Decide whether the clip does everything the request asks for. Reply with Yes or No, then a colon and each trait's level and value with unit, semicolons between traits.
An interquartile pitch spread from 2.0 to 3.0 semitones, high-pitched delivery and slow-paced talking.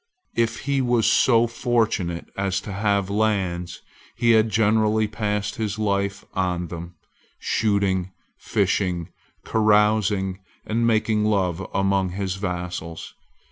No: average, 2.7 semitones; low, 100 Hz; slow, 115 wpm